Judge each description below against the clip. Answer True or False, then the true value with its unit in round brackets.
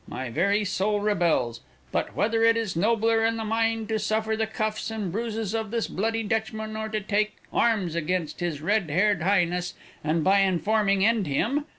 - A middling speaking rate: True (185 wpm)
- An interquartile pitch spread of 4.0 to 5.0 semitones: False (3.5 semitones)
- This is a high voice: True (210 Hz)